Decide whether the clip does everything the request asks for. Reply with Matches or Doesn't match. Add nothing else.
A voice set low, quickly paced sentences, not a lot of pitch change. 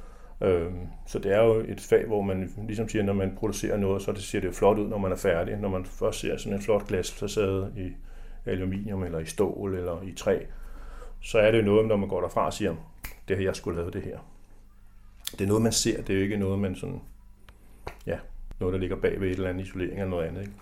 Matches